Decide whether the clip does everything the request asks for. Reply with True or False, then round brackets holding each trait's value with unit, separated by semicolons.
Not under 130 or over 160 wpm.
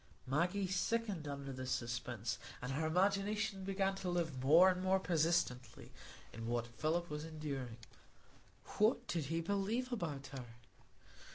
True (140 wpm)